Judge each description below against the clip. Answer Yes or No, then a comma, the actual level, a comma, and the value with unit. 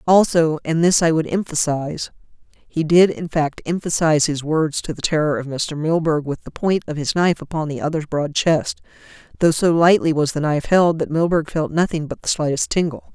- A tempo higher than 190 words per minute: Yes, average, 200 wpm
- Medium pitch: Yes, medium, 160 Hz